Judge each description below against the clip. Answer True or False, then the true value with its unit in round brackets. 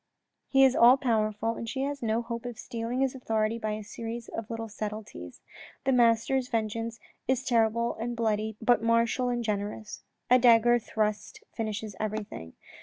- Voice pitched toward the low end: False (230 Hz)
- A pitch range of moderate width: False (1.8 semitones)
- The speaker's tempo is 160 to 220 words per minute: True (165 wpm)